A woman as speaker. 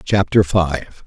No: male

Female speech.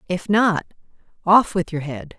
Yes: female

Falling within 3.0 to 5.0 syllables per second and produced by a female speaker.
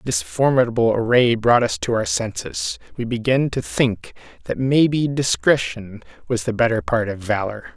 No: 4.7 syllables/s; male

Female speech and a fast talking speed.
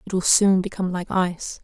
Yes: female; fast, 220 wpm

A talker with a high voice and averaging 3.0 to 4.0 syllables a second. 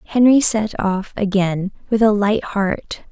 Yes: high, 205 Hz; 3.7 syllables/s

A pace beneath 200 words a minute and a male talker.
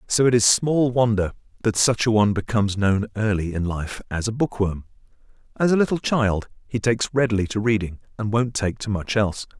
No: fast, 205 wpm; male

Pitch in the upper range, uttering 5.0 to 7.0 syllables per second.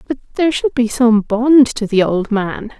No: high, 240 Hz; 4.6 syllables/s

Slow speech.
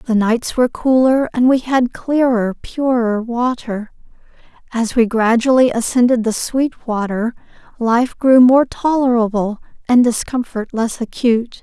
Yes: slow, 125 wpm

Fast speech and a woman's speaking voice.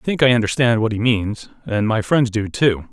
No: fast, 225 wpm; male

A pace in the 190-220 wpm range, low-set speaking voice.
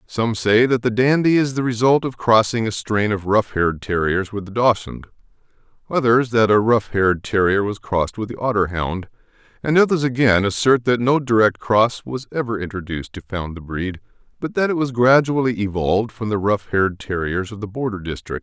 Yes: average, 195 wpm; low, 110 Hz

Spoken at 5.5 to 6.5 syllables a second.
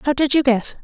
No: 5.3 syllables/s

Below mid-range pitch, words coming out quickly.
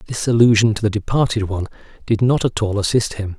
Yes: low, 110 Hz; fast, 215 wpm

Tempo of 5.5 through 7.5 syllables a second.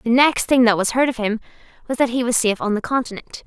Yes: 6.4 syllables/s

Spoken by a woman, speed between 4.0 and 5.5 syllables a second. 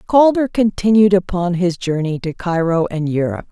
Yes: female; 5.0 syllables/s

